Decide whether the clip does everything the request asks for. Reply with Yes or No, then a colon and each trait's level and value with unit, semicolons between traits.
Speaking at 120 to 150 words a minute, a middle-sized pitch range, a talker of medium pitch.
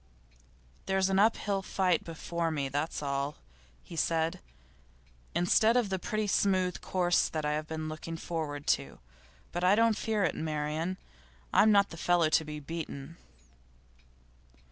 Yes: average, 145 wpm; average, 3.6 semitones; medium, 170 Hz